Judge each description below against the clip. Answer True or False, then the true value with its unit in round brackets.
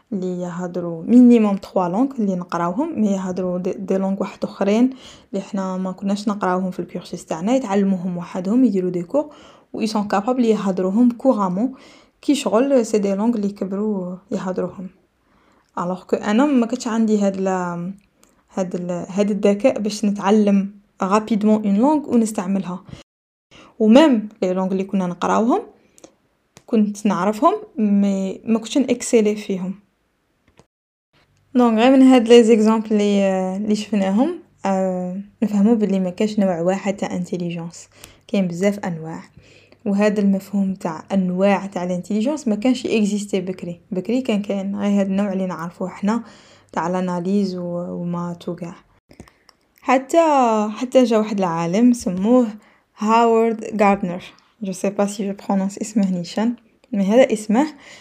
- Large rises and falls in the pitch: False (3.5 semitones)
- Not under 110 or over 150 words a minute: True (130 wpm)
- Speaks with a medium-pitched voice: False (205 Hz)